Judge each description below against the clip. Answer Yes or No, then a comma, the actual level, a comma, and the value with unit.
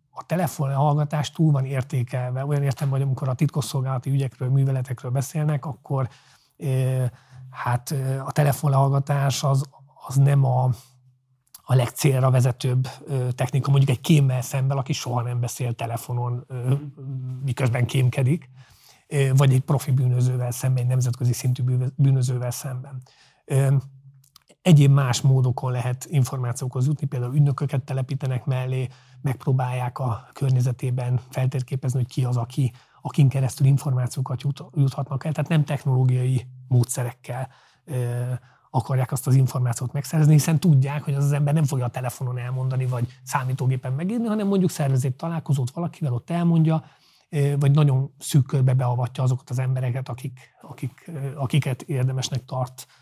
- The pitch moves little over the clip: Yes, narrow, 1.7 semitones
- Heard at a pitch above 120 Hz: Yes, low, 130 Hz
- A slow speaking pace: No, average, 130 wpm